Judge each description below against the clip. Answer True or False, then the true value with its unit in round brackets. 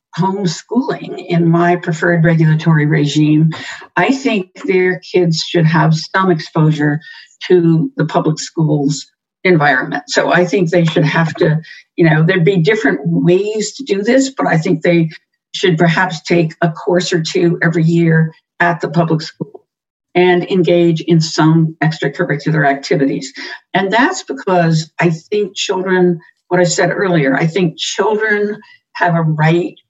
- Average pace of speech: True (150 wpm)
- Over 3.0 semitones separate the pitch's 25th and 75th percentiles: False (2.6 semitones)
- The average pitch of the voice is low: False (170 Hz)